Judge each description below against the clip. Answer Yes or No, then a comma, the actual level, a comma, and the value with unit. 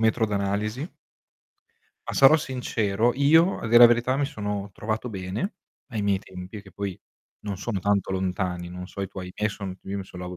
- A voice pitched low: Yes, low, 100 Hz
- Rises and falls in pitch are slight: No, average, 3.8 semitones